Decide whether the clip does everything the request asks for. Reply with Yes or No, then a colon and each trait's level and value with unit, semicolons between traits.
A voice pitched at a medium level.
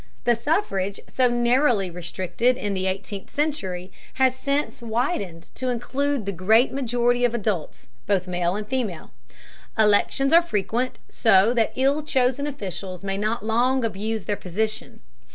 No: high, 225 Hz